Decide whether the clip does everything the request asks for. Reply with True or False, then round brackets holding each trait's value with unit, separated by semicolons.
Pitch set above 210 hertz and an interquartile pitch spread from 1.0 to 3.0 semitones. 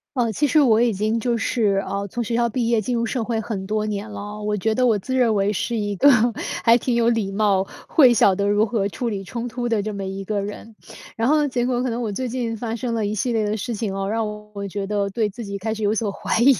True (220 Hz; 2.6 semitones)